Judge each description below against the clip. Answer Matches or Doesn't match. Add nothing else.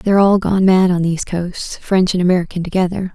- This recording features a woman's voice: Matches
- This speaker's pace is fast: Doesn't match